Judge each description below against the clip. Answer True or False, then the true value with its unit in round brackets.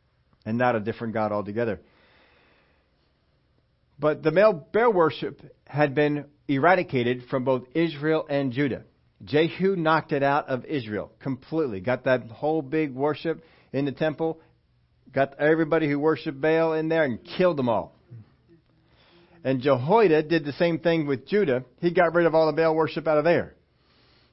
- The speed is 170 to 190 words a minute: False (160 wpm)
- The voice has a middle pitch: True (150 Hz)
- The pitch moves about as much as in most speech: True (4.3 semitones)